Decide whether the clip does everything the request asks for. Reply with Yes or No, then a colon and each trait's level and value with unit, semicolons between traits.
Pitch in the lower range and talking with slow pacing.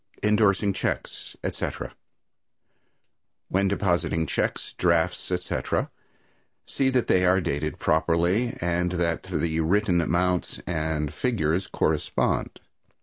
Yes: very low, 90 Hz; slow, 100 wpm